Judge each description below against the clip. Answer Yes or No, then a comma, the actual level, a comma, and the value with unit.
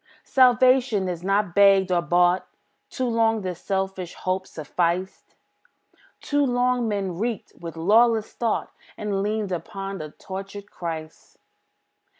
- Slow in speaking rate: Yes, slow, 125 wpm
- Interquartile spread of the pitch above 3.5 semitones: Yes, average, 3.9 semitones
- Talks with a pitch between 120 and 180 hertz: No, high, 195 Hz